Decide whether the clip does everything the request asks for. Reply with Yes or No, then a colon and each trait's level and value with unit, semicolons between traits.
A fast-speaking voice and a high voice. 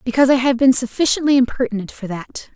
No: average, 190 wpm; very high, 250 Hz